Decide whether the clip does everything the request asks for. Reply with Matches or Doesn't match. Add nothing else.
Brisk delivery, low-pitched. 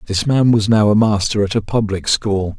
Matches